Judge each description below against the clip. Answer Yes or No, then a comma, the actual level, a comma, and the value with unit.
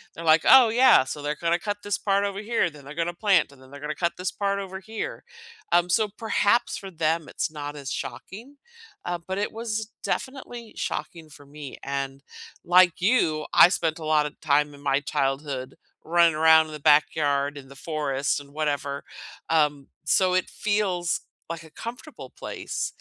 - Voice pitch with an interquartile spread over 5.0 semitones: Yes, wide, 5.4 semitones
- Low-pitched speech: No, medium, 160 Hz